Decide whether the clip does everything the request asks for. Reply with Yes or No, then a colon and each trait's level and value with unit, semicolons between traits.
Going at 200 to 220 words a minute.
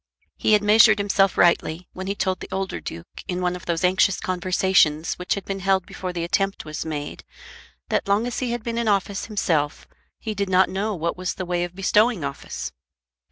Yes: fast, 205 wpm